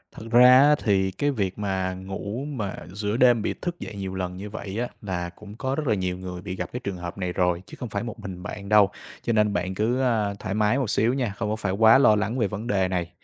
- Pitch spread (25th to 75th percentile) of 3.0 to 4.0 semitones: Yes, average, 3.6 semitones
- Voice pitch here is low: Yes, low, 105 Hz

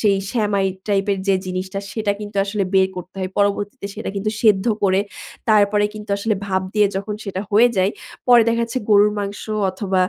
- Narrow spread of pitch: Yes, narrow, 1.5 semitones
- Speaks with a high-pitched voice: Yes, high, 200 Hz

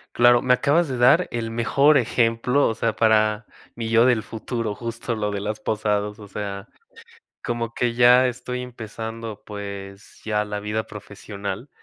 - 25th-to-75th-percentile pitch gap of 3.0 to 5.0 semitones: No, narrow, 2.6 semitones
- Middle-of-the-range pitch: No, low, 115 Hz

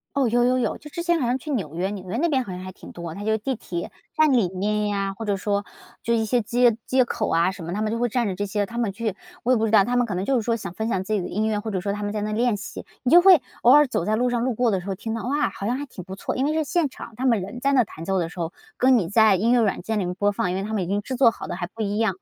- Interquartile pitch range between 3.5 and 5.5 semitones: Yes, average, 4.0 semitones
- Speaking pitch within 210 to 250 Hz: Yes, high, 220 Hz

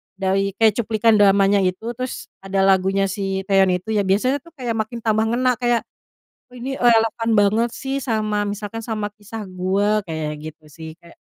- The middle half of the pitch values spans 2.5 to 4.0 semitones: Yes, average, 2.9 semitones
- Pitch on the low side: No, high, 210 Hz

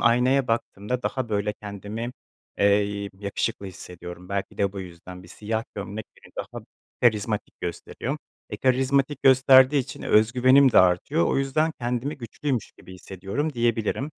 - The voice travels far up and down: No, average, 4.6 semitones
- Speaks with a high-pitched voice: No, low, 115 Hz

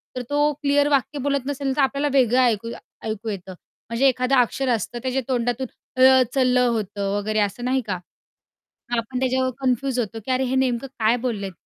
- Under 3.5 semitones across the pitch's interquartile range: Yes, average, 2.8 semitones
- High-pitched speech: Yes, very high, 255 Hz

